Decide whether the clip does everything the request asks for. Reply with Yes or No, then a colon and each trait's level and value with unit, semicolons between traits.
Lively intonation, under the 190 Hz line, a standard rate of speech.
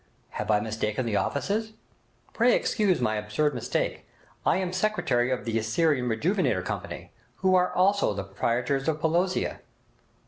Yes: wide, 8.7 semitones; medium, 140 Hz; average, 145 wpm